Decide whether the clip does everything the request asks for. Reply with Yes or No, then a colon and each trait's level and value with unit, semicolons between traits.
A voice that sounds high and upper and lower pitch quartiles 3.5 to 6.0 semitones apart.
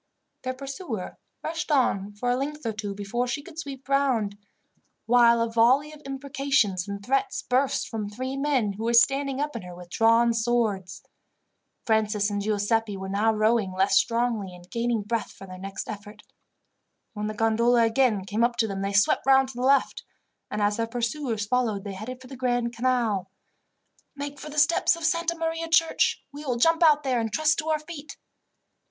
Yes: high, 235 Hz; average, 4.7 semitones